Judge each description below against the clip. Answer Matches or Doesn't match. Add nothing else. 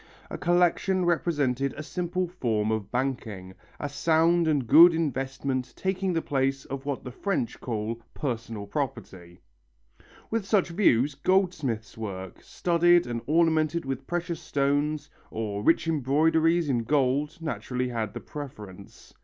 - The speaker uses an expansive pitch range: Matches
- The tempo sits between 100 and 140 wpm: Matches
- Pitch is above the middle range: Doesn't match